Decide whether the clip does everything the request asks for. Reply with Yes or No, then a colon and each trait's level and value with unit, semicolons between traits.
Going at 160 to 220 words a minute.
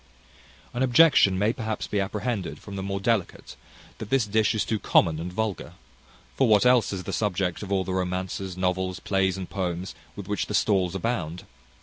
Yes: average, 190 wpm